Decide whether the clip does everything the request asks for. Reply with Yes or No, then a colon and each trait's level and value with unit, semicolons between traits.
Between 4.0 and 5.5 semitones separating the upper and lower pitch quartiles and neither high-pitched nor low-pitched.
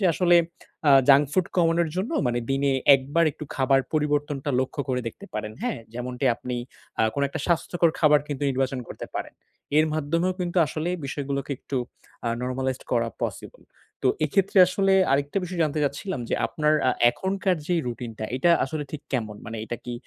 Yes: average, 4.3 semitones; medium, 145 Hz